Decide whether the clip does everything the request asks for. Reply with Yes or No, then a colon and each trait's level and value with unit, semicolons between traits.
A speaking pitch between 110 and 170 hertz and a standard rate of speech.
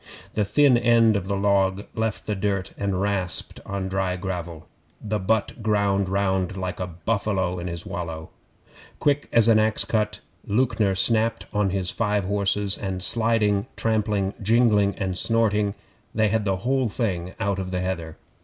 No: low, 100 Hz; average, 165 wpm